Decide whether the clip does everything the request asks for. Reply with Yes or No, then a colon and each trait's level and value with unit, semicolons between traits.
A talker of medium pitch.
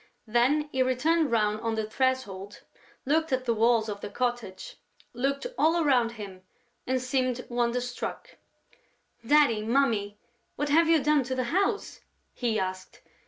No: very high, 250 Hz